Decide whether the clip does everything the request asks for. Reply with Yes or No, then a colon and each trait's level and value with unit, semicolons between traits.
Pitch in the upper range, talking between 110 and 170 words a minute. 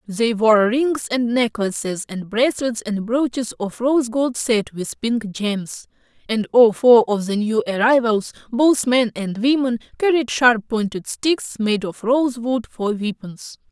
Yes: high, 235 Hz; average, 155 wpm